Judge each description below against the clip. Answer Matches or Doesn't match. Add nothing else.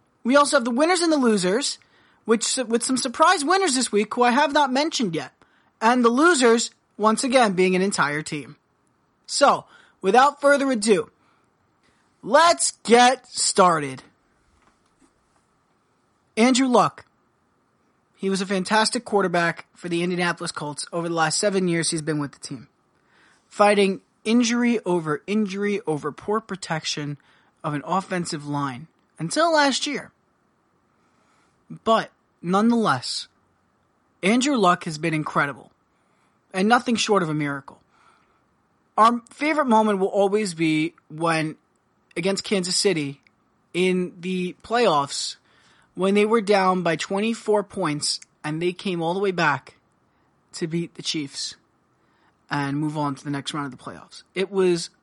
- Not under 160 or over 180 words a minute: Doesn't match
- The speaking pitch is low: Doesn't match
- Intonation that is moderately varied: Doesn't match